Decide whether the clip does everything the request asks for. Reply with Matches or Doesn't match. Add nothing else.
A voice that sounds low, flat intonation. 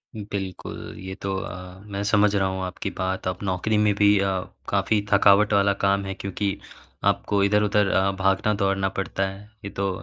Matches